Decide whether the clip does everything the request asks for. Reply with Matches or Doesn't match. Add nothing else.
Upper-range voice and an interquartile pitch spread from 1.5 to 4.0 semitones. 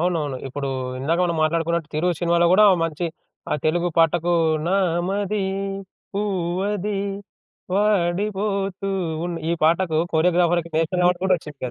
Doesn't match